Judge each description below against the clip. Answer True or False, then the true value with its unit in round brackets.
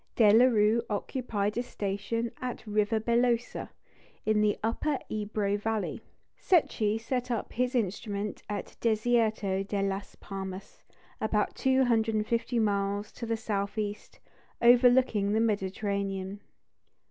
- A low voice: False (215 Hz)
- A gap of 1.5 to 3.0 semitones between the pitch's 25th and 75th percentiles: True (2.5 semitones)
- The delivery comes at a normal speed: False (115 wpm)